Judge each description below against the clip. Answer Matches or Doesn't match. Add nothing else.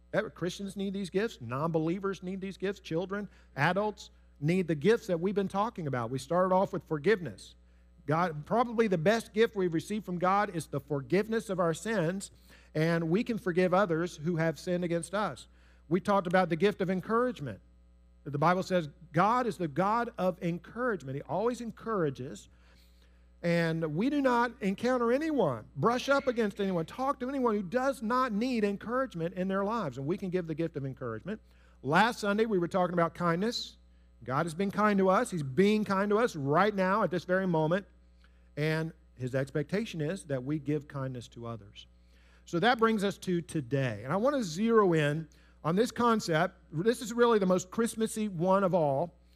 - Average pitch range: Doesn't match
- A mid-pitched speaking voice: Matches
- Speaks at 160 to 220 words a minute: Matches